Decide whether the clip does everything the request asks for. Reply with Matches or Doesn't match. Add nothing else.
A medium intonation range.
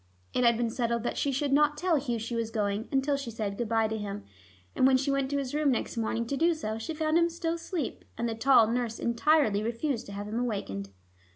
Matches